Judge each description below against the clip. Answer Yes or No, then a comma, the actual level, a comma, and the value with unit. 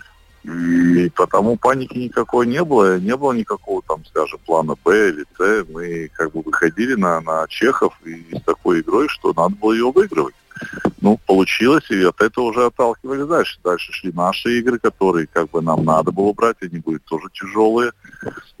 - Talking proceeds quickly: Yes, fast, 175 wpm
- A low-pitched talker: Yes, low, 100 Hz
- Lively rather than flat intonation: Yes, wide, 6.2 semitones